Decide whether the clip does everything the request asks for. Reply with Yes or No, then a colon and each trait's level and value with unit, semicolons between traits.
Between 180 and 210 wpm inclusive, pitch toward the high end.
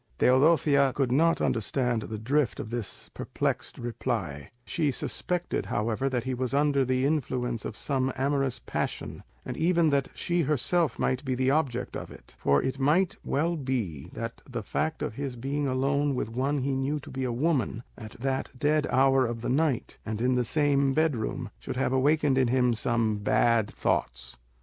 No: average, 185 wpm; low, 130 Hz